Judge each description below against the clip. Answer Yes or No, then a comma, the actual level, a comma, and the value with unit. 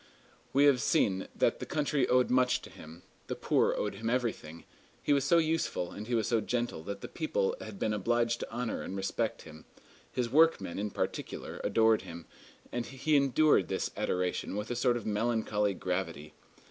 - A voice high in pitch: No, low, 115 Hz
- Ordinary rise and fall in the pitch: Yes, average, 4.6 semitones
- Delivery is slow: No, average, 185 wpm